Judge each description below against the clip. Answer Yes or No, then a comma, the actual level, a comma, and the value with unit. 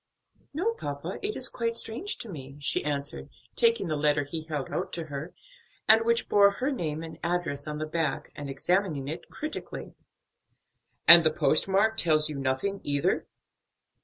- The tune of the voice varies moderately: No, wide, 5.9 semitones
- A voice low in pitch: No, medium, 165 Hz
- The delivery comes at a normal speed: Yes, average, 170 wpm